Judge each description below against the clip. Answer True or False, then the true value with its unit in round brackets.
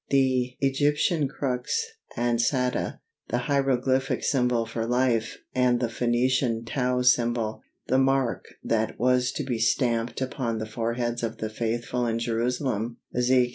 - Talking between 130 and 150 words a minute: True (135 wpm)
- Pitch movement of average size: False (1.9 semitones)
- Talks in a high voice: False (125 Hz)